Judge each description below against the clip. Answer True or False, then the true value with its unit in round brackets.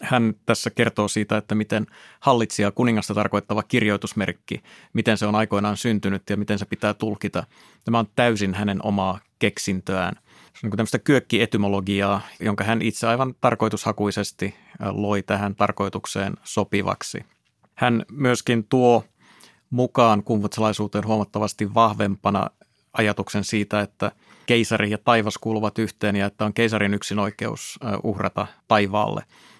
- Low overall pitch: True (105 Hz)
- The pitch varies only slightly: True (1.9 semitones)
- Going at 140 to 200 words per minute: False (130 wpm)